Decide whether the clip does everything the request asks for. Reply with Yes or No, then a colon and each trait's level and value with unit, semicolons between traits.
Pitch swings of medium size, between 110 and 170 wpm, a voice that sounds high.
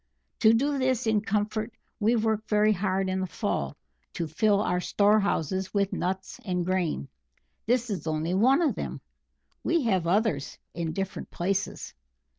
Yes: average, 3.4 semitones; average, 155 wpm; high, 200 Hz